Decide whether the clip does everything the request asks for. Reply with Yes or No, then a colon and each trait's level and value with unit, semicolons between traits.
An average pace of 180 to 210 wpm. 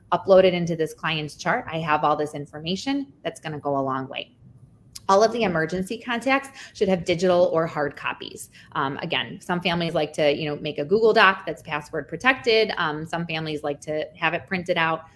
Yes: fast, 205 wpm